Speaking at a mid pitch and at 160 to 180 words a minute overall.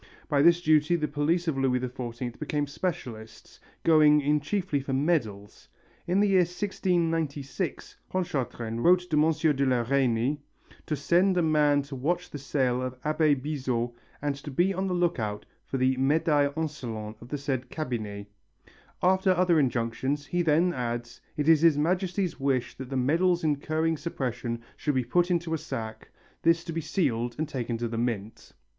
Yes: medium, 145 Hz; average, 170 wpm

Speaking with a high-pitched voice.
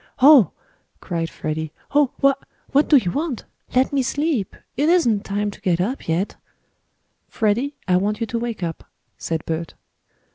Yes: high, 220 Hz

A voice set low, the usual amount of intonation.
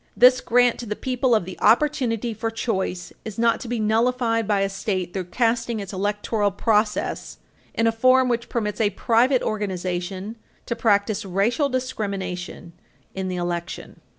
No: high, 220 Hz; average, 3.3 semitones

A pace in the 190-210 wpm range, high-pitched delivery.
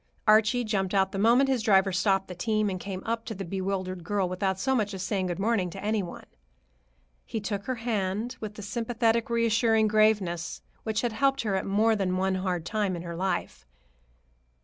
Yes: average, 200 wpm; high, 205 Hz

